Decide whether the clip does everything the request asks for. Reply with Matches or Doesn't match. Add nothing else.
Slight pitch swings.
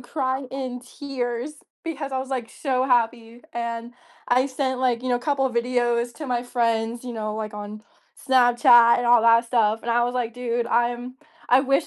Matches